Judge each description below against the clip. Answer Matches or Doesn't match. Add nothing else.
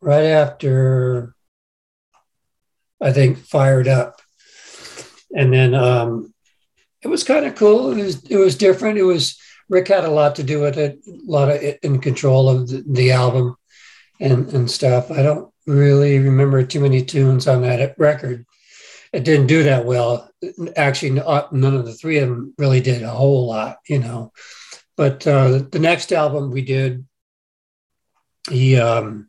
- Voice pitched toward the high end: Doesn't match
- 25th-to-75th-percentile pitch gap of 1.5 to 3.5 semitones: Matches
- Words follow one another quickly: Doesn't match